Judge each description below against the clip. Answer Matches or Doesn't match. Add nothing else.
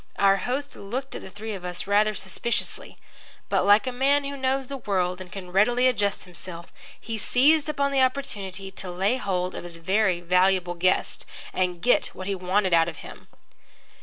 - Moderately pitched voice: Doesn't match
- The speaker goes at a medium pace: Matches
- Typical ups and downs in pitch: Doesn't match